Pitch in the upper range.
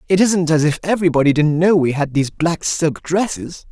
No: medium, 165 Hz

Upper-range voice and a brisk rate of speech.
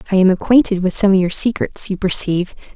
Yes: high, 195 Hz; fast, 220 wpm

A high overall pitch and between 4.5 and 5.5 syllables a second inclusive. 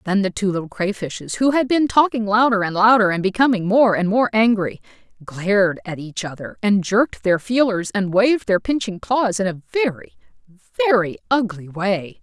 Yes: high, 205 Hz; 5.0 syllables/s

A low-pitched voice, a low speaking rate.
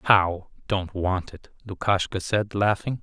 Yes: low, 100 Hz; slow, 120 wpm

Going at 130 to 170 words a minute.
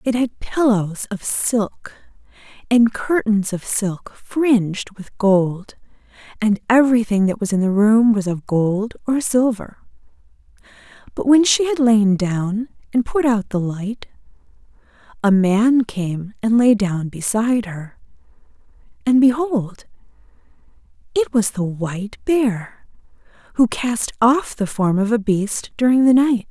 Yes: average, 140 wpm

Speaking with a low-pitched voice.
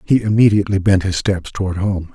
Yes: low, 100 Hz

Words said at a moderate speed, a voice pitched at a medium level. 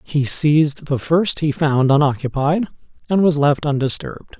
Yes: average, 150 wpm; medium, 150 Hz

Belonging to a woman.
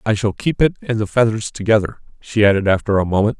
No: male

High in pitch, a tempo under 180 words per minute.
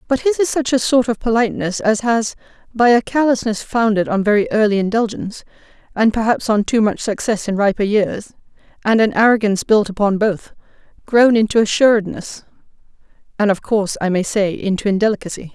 Yes: high, 215 Hz; average, 170 wpm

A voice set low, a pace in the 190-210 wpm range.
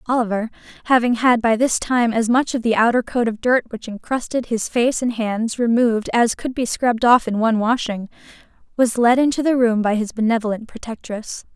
No: high, 235 Hz; average, 195 wpm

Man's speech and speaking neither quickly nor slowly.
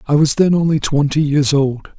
No: male; fast, 210 wpm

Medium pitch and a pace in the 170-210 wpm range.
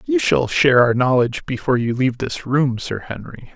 No: low, 130 Hz; fast, 205 wpm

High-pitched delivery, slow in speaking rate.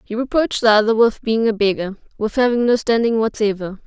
No: high, 225 Hz; average, 200 wpm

